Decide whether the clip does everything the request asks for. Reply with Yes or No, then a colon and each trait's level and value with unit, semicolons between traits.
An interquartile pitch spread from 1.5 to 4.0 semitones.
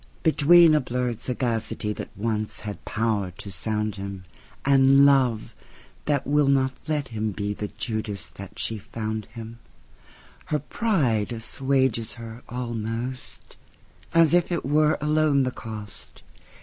No: average, 4.5 semitones